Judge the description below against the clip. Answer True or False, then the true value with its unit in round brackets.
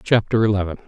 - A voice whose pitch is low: True (105 Hz)